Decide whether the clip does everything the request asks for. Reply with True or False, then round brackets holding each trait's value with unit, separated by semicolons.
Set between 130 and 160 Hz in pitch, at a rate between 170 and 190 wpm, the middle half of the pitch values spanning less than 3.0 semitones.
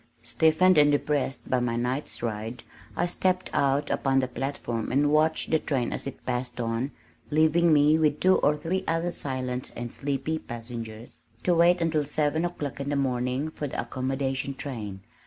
False (140 Hz; 175 wpm; 4.0 semitones)